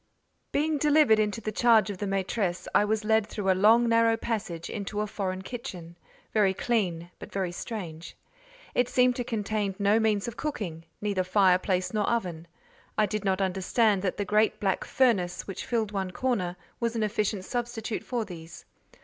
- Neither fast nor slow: Yes, average, 175 wpm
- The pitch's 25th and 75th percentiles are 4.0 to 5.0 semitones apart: No, average, 3.4 semitones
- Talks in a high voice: Yes, high, 210 Hz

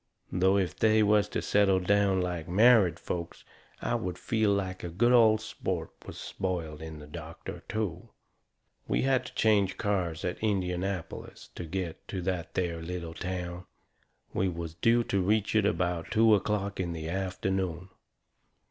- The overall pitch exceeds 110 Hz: No, very low, 95 Hz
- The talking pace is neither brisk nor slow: Yes, average, 160 wpm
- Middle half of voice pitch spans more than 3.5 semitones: No, average, 2.9 semitones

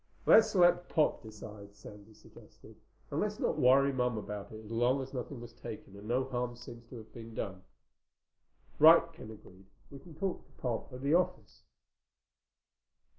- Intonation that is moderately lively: Yes, average, 4.4 semitones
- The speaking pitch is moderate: No, low, 120 Hz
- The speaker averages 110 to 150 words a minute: No, average, 175 wpm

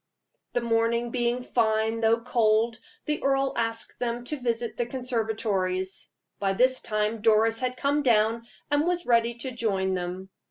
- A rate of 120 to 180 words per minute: Yes, average, 155 wpm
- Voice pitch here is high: Yes, high, 230 Hz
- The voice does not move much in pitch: Yes, narrow, 2.2 semitones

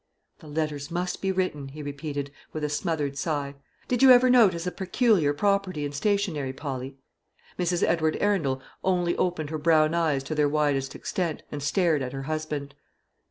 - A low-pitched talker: No, medium, 155 Hz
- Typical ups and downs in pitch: Yes, average, 3.9 semitones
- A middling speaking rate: Yes, average, 170 wpm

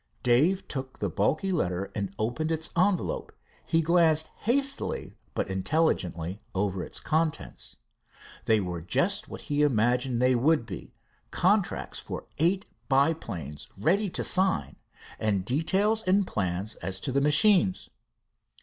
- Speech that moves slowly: Yes, slow, 130 wpm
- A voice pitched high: No, medium, 140 Hz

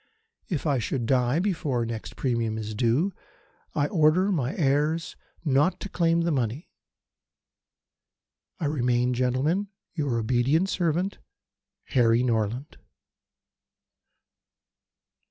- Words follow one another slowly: Yes, slow, 105 wpm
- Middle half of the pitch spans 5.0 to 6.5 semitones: Yes, wide, 5.4 semitones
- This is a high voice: No, low, 135 Hz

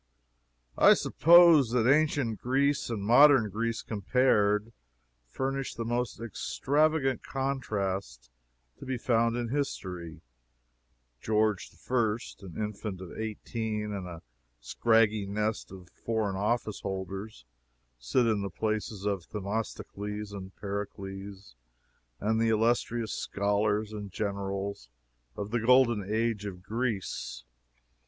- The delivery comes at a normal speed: No, slow, 110 wpm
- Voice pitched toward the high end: No, low, 110 Hz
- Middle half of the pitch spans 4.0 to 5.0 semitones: No, average, 3.1 semitones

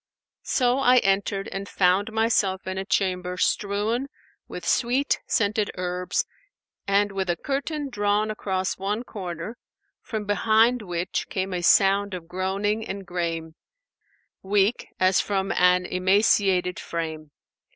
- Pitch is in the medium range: No, high, 195 Hz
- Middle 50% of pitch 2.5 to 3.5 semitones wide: Yes, average, 2.8 semitones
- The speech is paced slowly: Yes, slow, 130 wpm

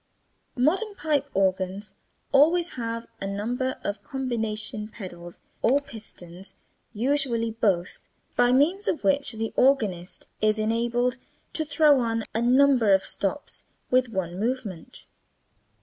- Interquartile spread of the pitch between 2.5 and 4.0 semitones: No, average, 4.9 semitones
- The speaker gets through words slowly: Yes, slow, 120 wpm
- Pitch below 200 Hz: No, high, 230 Hz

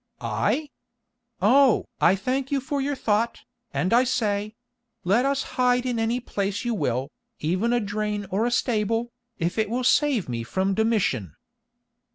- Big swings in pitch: No, average, 3.8 semitones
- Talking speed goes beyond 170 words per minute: No, average, 155 wpm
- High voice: Yes, high, 225 Hz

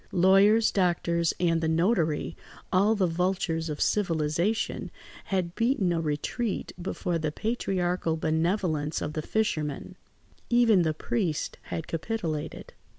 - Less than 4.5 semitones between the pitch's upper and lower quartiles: Yes, average, 3.8 semitones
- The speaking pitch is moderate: Yes, medium, 175 Hz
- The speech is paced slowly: Yes, slow, 120 wpm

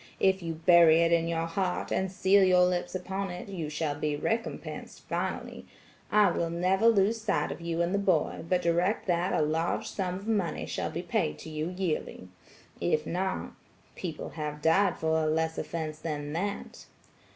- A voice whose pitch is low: No, medium, 170 Hz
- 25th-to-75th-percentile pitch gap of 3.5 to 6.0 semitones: No, average, 3.0 semitones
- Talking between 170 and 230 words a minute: Yes, average, 175 wpm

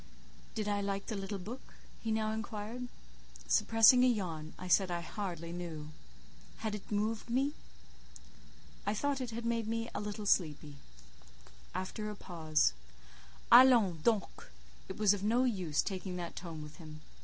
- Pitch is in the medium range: No, high, 205 Hz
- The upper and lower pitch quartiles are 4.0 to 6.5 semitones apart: Yes, average, 4.5 semitones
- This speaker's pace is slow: No, average, 155 wpm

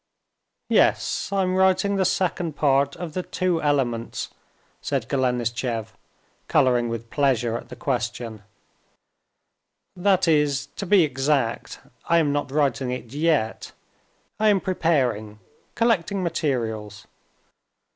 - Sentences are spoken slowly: Yes, slow, 110 wpm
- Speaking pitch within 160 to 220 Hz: No, medium, 140 Hz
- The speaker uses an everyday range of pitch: No, wide, 6.5 semitones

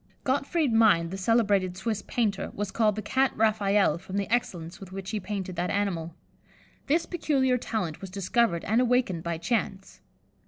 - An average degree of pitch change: Yes, average, 4.0 semitones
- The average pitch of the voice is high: Yes, high, 205 Hz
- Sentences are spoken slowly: No, average, 170 wpm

